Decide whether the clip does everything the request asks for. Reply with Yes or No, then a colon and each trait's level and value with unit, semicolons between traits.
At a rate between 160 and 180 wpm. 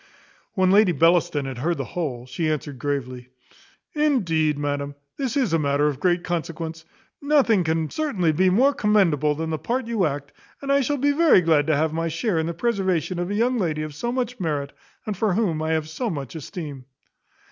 No: average, 200 wpm